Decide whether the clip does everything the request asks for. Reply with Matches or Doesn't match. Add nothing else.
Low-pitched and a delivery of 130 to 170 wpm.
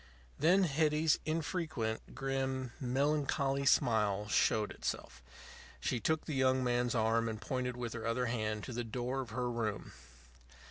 Matches